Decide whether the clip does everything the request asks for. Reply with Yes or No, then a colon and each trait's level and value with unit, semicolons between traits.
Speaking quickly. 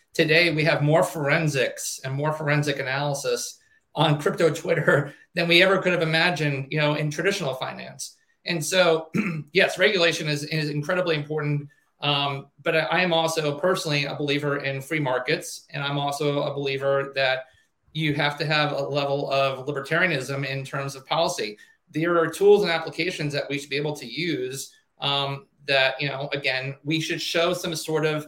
No: average, 175 wpm